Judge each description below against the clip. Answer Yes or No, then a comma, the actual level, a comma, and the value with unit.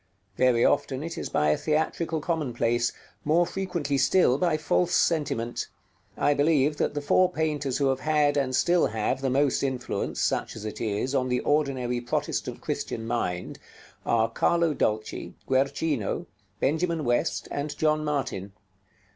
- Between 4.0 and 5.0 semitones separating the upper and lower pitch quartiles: Yes, average, 4.3 semitones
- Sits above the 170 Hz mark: No, medium, 140 Hz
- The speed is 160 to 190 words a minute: No, average, 150 wpm